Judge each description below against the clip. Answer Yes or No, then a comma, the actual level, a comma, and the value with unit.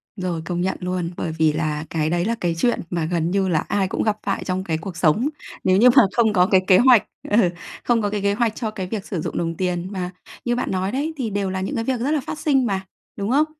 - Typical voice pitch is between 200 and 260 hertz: No, high, 190 Hz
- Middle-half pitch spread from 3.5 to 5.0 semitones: Yes, average, 4.4 semitones